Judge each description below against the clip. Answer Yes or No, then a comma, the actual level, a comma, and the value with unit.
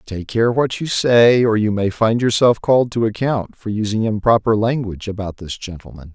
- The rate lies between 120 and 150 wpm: No, average, 195 wpm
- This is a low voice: Yes, low, 110 Hz